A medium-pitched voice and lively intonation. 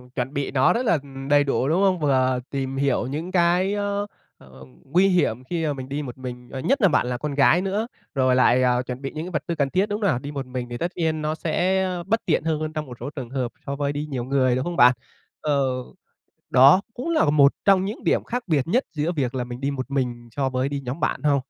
No: medium, 145 Hz; average, 5.0 semitones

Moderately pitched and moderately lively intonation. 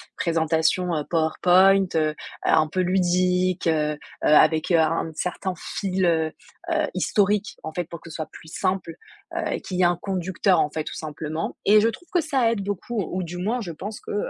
Yes: medium, 180 Hz; average, 3.3 semitones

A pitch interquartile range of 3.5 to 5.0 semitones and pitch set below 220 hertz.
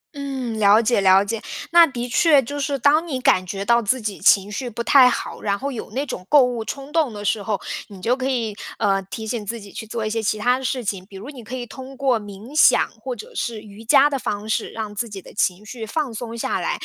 No: average, 4.1 semitones; high, 230 Hz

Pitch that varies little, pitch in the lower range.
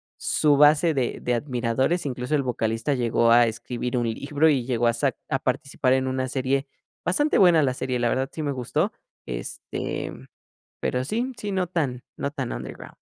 No: average, 3.5 semitones; low, 130 Hz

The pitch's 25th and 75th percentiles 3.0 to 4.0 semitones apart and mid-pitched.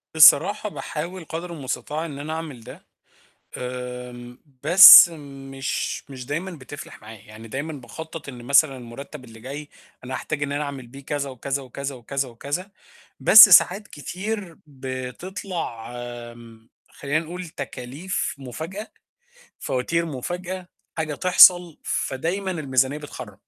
No: average, 4.6 semitones; medium, 145 Hz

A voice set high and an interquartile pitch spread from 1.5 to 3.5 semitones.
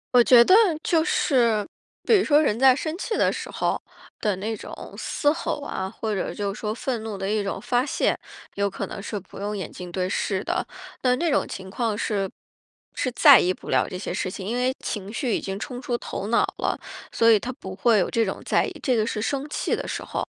No: high, 220 Hz; average, 4.2 semitones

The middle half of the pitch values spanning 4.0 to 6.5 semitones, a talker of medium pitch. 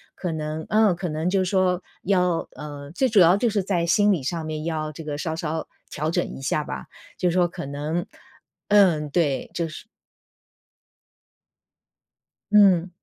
No: average, 3.3 semitones; medium, 170 Hz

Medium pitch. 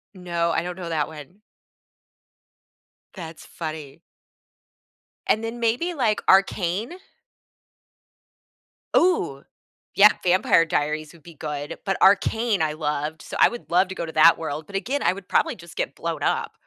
Yes: medium, 170 Hz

